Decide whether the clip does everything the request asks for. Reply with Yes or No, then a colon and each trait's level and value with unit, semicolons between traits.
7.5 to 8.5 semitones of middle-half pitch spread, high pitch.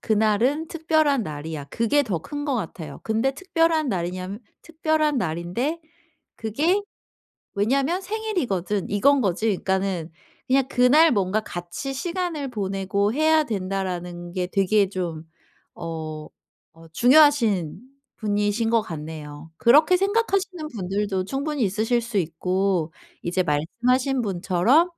Yes: wide, 8.1 semitones; high, 215 Hz